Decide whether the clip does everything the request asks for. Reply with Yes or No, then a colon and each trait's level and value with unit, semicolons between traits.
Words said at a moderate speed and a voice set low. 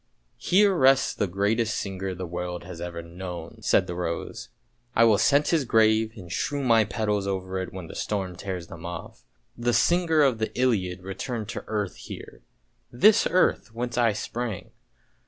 Yes: average, 190 wpm; low, 105 Hz